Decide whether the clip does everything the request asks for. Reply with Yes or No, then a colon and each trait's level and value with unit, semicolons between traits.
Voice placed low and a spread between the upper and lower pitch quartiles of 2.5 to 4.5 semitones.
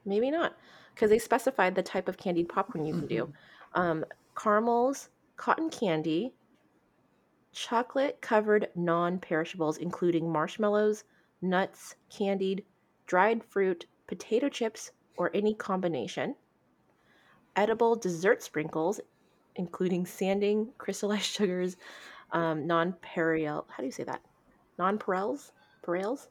No: high, 190 Hz; average, 3.9 semitones